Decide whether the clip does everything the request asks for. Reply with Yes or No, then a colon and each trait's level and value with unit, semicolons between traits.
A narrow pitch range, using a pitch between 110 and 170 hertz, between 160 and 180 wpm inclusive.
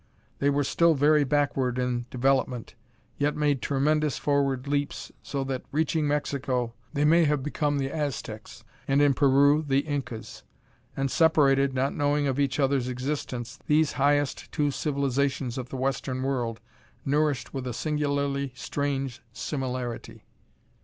No: narrow, 2.0 semitones; medium, 140 Hz; average, 140 wpm